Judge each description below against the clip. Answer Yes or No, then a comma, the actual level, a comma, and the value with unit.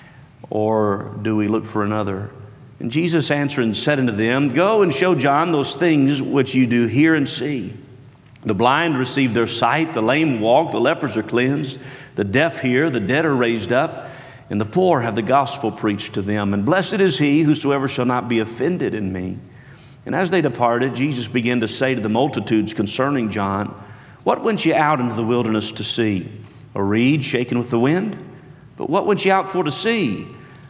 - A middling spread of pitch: Yes, average, 4.7 semitones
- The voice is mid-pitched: No, low, 130 Hz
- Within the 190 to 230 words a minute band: Yes, average, 195 wpm